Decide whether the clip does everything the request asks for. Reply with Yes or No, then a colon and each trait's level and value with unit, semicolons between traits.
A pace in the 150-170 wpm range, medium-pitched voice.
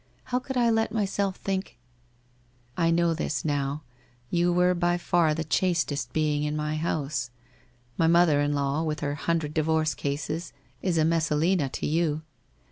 Yes: average, 160 wpm; medium, 160 Hz